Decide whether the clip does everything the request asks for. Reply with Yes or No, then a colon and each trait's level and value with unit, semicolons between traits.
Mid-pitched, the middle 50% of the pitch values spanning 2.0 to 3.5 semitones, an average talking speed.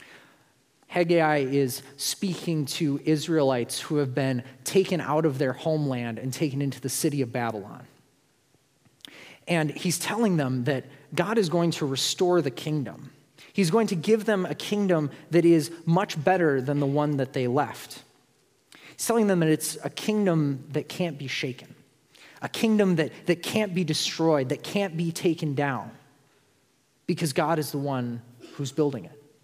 No: medium, 150 Hz; average, 4.0 semitones; average, 165 wpm